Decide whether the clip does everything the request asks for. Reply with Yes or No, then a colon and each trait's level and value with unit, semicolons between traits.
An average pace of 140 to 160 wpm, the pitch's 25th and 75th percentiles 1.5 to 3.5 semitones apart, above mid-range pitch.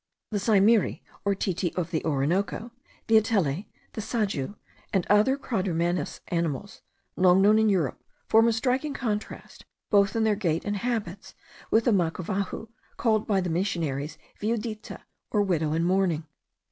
No: average, 145 wpm; average, 4.1 semitones; high, 200 Hz